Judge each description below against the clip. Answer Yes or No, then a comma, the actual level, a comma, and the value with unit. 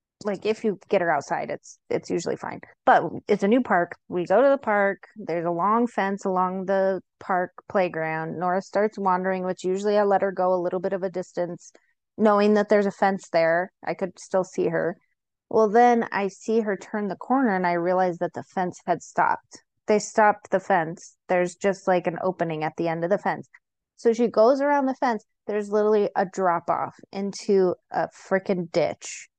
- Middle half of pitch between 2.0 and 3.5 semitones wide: Yes, narrow, 2.6 semitones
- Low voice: No, high, 195 Hz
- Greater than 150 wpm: Yes, fast, 205 wpm